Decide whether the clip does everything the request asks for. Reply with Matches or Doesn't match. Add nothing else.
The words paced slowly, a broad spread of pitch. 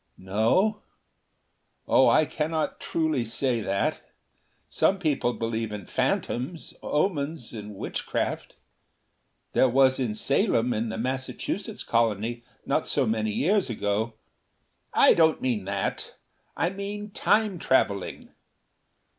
Matches